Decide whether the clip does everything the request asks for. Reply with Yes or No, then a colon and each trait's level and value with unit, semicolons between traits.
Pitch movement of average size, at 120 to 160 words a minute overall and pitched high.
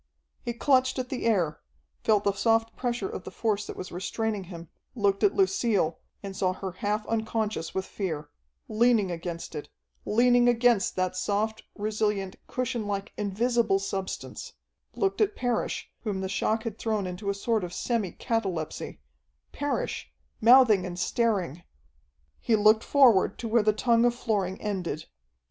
Yes: average, 3.6 semitones; average, 155 wpm; high, 215 Hz